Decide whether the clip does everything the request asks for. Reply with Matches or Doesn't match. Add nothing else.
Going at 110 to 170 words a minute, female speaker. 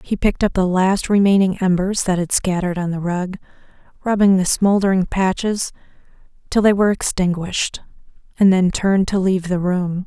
Matches